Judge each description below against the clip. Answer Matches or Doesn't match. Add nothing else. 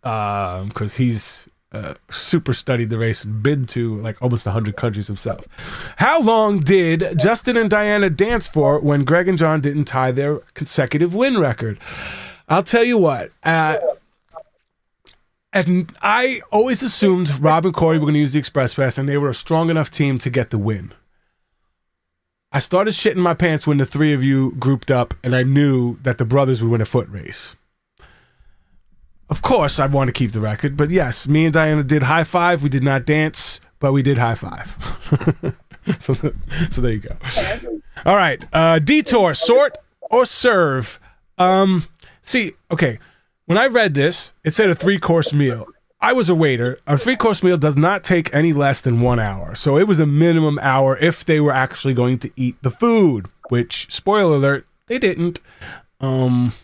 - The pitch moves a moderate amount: Doesn't match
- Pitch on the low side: Doesn't match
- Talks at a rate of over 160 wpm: Matches